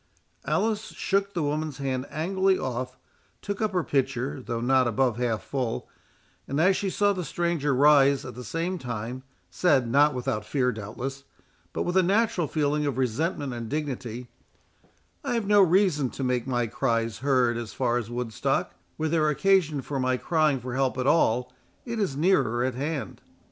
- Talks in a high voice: No, low, 135 Hz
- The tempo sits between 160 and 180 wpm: Yes, average, 175 wpm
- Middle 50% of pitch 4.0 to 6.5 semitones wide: Yes, average, 5.0 semitones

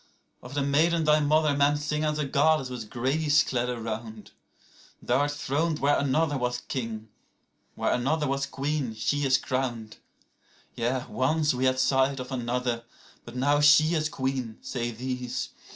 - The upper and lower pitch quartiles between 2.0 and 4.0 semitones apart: Yes, average, 3.1 semitones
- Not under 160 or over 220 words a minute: No, average, 150 wpm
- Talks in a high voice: No, low, 135 Hz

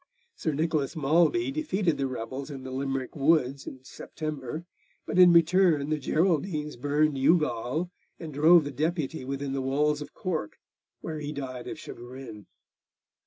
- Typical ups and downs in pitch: Yes, average, 3.3 semitones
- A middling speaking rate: Yes, average, 150 wpm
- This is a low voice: No, medium, 150 Hz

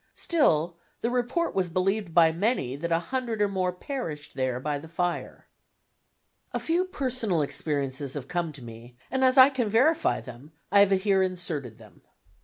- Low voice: No, medium, 180 Hz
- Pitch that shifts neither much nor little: No, wide, 8.0 semitones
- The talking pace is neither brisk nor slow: Yes, average, 175 wpm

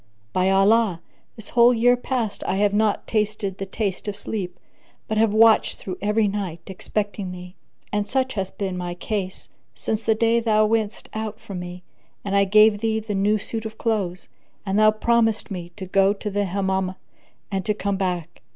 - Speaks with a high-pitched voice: Yes, high, 205 Hz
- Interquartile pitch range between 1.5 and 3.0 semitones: Yes, narrow, 2.4 semitones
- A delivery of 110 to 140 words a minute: No, average, 190 wpm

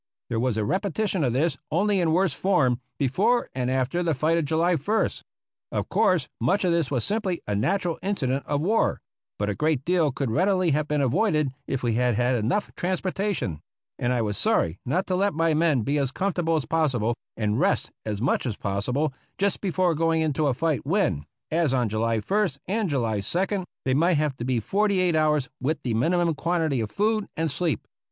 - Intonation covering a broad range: Yes, wide, 6.3 semitones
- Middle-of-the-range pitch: Yes, medium, 155 Hz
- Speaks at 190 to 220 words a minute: Yes, average, 200 wpm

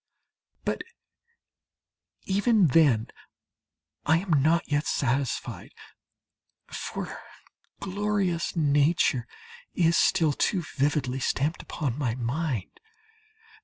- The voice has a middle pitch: Yes, medium, 150 Hz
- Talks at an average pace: No, slow, 85 wpm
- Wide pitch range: No, average, 4.3 semitones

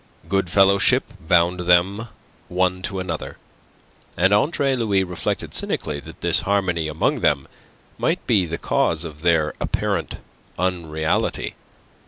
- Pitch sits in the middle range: No, very low, 90 Hz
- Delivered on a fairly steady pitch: No, average, 3.0 semitones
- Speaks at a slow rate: Yes, slow, 125 wpm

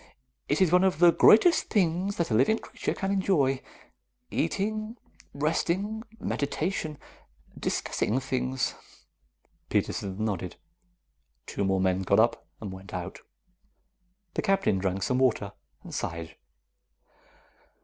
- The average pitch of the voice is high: No, low, 135 Hz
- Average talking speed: No, slow, 120 wpm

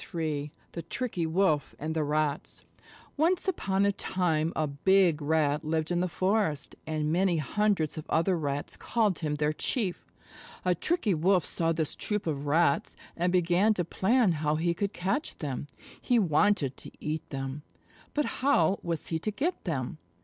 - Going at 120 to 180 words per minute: Yes, average, 170 wpm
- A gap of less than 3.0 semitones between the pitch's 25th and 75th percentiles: No, average, 4.3 semitones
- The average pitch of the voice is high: No, medium, 165 Hz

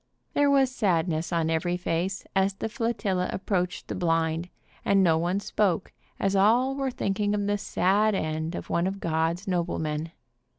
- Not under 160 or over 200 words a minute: Yes, average, 170 wpm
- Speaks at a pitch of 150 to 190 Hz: Yes, medium, 185 Hz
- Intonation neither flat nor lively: Yes, average, 3.6 semitones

